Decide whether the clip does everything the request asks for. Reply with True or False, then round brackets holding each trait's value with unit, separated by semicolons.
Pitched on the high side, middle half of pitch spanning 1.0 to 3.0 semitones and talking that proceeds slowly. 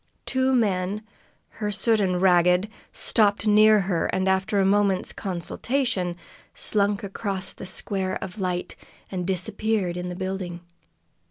True (195 Hz; 2.4 semitones; 125 wpm)